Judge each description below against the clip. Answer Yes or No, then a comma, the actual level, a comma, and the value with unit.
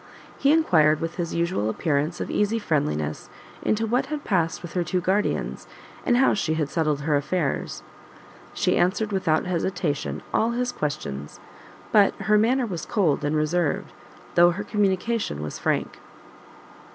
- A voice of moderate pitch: Yes, medium, 175 Hz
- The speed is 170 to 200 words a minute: No, average, 150 wpm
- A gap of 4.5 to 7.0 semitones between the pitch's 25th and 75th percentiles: Yes, wide, 5.4 semitones